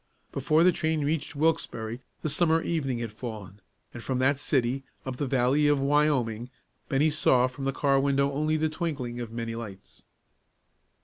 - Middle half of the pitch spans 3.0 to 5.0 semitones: Yes, average, 3.9 semitones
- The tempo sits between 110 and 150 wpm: No, average, 170 wpm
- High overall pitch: No, low, 135 Hz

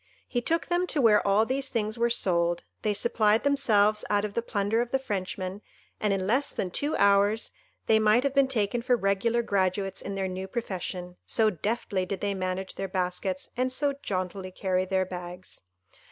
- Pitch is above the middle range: Yes, high, 205 Hz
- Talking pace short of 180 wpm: No, average, 190 wpm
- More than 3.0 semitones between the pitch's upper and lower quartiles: Yes, average, 4.0 semitones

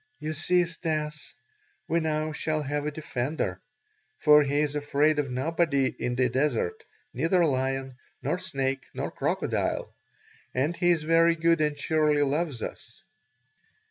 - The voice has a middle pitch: Yes, medium, 150 Hz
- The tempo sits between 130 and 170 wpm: Yes, average, 140 wpm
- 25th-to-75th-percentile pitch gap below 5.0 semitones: Yes, average, 3.0 semitones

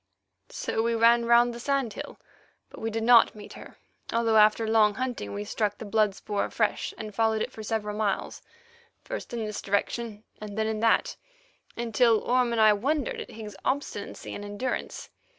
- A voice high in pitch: Yes, high, 220 Hz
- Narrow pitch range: Yes, narrow, 2.0 semitones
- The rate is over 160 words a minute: Yes, average, 185 wpm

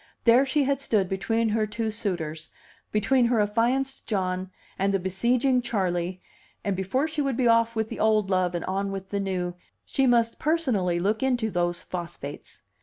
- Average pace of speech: Yes, average, 180 wpm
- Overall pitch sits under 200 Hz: No, high, 210 Hz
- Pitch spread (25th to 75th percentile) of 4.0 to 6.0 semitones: Yes, average, 4.5 semitones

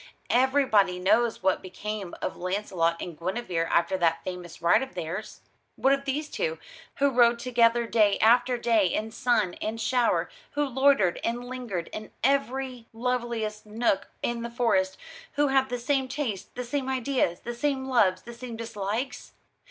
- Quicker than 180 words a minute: No, average, 160 wpm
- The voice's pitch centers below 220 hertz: No, high, 235 Hz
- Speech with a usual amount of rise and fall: Yes, average, 4.7 semitones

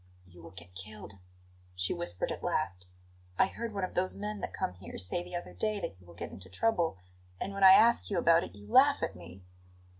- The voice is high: No, low, 105 Hz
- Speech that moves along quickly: Yes, fast, 230 wpm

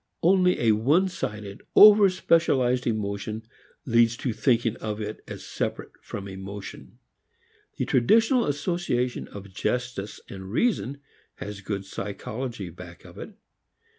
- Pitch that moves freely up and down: Yes, wide, 5.8 semitones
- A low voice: Yes, low, 115 Hz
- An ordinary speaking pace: No, slow, 125 wpm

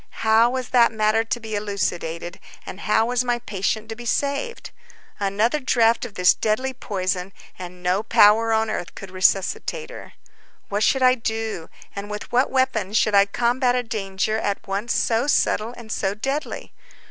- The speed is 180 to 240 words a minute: No, average, 170 wpm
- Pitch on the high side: Yes, high, 220 Hz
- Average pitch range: Yes, average, 3.4 semitones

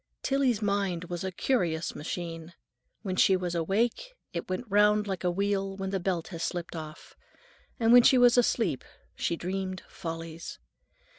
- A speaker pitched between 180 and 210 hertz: Yes, high, 190 Hz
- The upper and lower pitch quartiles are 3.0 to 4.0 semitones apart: Yes, average, 3.3 semitones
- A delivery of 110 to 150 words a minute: No, average, 160 wpm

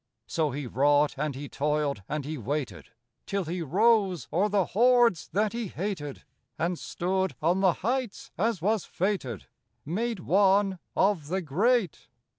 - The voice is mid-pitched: Yes, medium, 180 Hz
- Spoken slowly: No, average, 150 wpm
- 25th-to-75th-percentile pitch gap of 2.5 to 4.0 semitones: No, wide, 5.5 semitones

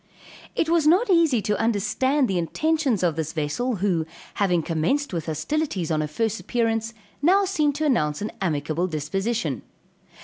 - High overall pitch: Yes, high, 210 Hz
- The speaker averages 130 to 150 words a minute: No, average, 160 wpm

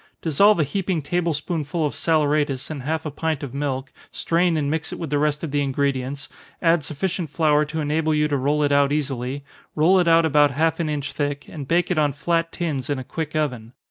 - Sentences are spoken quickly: Yes, fast, 225 wpm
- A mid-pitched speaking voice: Yes, medium, 150 Hz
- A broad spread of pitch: No, narrow, 2.4 semitones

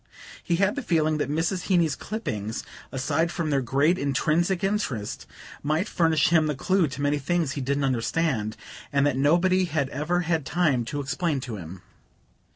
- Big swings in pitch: No, average, 4.2 semitones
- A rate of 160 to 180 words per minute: Yes, average, 170 wpm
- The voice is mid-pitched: Yes, medium, 155 Hz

